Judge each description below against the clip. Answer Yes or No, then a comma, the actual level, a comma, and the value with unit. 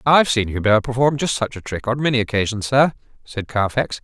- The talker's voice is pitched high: No, low, 120 Hz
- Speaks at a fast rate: Yes, fast, 225 wpm